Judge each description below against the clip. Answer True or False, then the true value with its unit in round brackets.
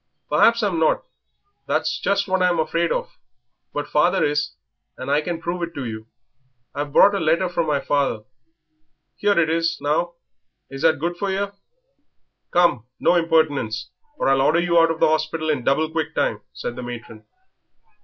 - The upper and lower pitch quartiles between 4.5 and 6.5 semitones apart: False (3.3 semitones)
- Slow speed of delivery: False (175 wpm)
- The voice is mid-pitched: True (160 Hz)